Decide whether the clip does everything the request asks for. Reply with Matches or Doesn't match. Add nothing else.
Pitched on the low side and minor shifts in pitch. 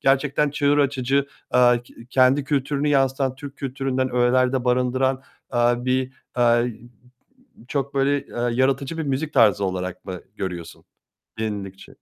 Matches